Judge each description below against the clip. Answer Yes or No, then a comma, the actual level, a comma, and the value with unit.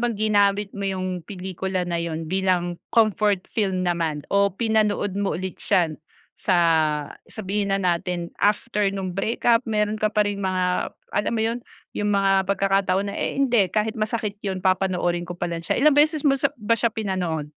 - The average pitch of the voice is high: Yes, high, 195 Hz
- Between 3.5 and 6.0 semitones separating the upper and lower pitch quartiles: No, average, 2.7 semitones